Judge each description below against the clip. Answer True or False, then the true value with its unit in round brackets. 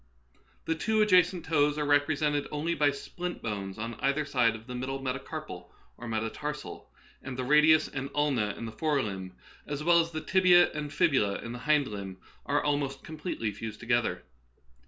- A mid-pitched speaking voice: True (145 Hz)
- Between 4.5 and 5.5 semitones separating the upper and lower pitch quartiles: True (4.9 semitones)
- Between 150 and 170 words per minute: False (185 wpm)